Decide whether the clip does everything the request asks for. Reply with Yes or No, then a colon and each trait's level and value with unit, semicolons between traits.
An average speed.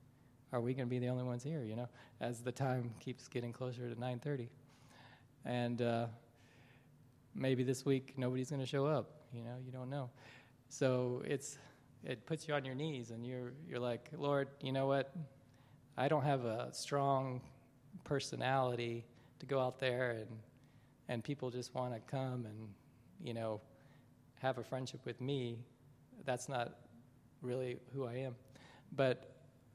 Yes: average, 165 wpm